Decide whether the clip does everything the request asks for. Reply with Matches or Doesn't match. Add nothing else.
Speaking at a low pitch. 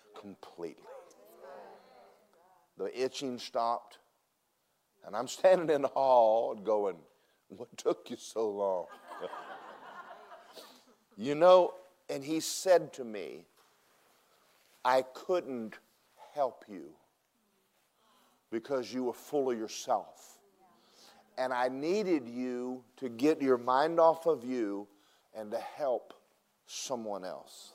Matches